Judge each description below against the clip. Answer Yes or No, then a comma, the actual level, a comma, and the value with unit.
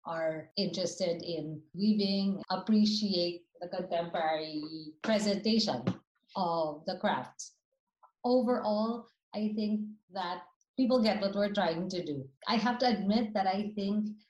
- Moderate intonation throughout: Yes, average, 3.7 semitones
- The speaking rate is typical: No, slow, 120 wpm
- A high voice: Yes, high, 195 Hz